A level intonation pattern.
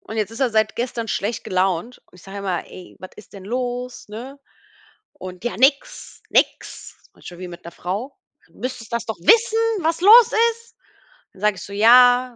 No: average, 4.6 semitones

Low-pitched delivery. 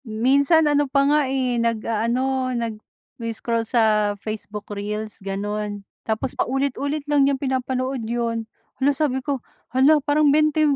No: very high, 255 Hz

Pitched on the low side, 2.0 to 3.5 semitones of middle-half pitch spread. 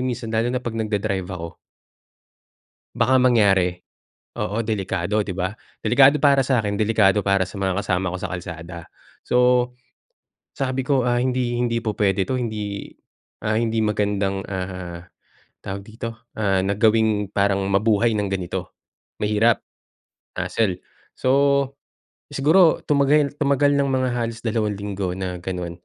No: low, 110 Hz; average, 4.2 semitones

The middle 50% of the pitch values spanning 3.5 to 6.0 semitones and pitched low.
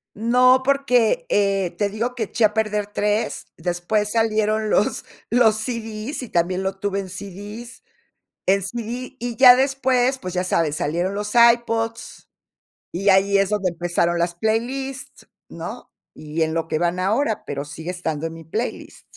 No: average, 4.5 semitones; high, 210 Hz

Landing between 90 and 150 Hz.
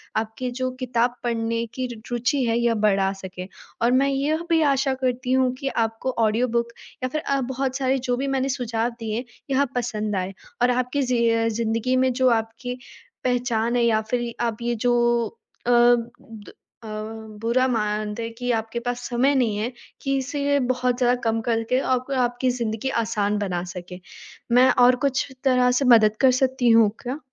No: high, 245 Hz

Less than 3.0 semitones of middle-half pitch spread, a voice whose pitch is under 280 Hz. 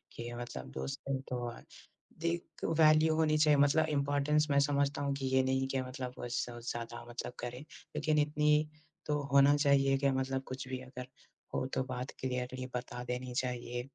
Yes: narrow, 2.5 semitones; low, 135 Hz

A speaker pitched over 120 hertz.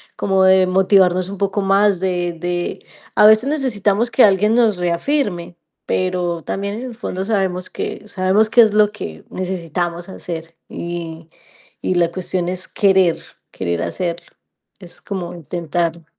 Yes: medium, 185 Hz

